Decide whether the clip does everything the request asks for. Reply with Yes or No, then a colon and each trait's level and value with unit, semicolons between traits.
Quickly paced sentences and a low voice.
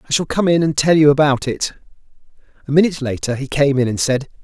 No: fast, 230 wpm; medium, 145 Hz